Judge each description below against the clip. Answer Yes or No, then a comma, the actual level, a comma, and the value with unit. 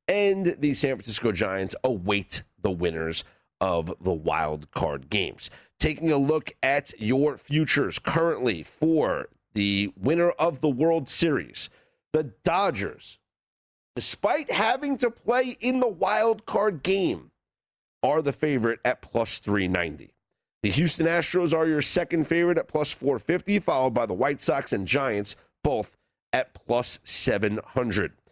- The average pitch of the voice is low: No, medium, 145 Hz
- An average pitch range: No, wide, 8.3 semitones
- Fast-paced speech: No, average, 140 wpm